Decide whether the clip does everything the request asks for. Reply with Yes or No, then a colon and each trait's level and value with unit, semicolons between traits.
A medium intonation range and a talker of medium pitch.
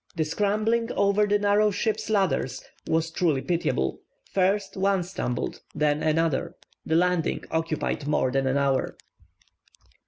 Yes: average, 4.8 semitones; medium, 180 Hz